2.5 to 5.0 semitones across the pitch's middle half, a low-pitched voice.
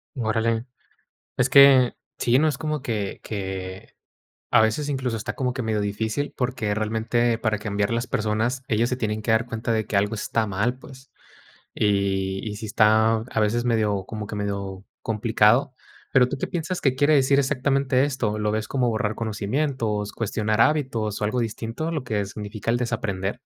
Yes: average, 3.3 semitones; low, 110 Hz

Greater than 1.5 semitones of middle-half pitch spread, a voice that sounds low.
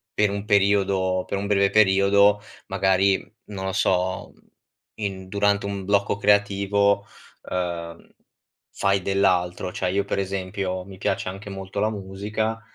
No: narrow, 1.2 semitones; low, 100 Hz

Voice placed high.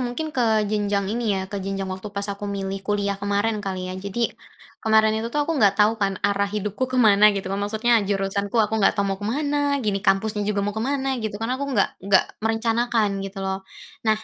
Yes: high, 210 Hz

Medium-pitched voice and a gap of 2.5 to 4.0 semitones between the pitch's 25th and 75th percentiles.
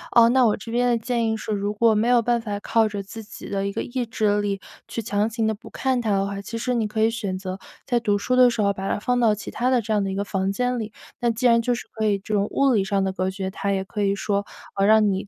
No: high, 215 Hz; average, 2.8 semitones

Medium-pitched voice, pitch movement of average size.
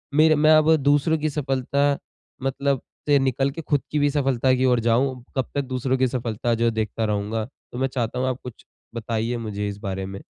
No: low, 130 Hz; average, 3.5 semitones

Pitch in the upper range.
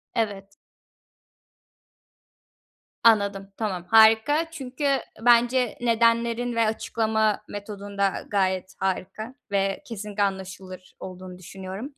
Yes: high, 210 Hz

